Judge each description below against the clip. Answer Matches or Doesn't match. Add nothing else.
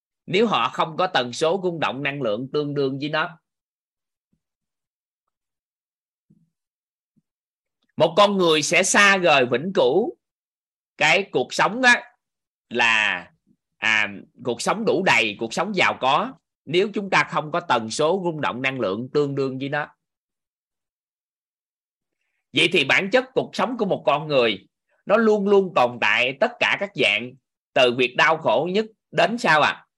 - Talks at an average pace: Doesn't match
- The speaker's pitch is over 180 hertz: Doesn't match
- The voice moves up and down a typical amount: Doesn't match